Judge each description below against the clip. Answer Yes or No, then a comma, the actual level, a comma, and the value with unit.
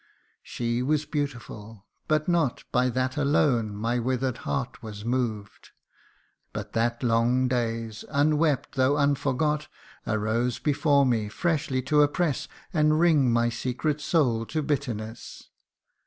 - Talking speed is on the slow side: Yes, slow, 125 wpm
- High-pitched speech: No, low, 130 Hz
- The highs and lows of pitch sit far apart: No, average, 4.1 semitones